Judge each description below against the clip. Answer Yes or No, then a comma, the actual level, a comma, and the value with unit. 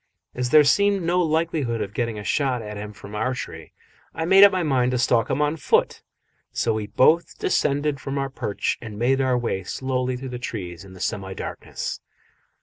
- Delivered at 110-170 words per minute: No, fast, 205 wpm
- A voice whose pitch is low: Yes, low, 125 Hz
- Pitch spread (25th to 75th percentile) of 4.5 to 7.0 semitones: Yes, wide, 5.6 semitones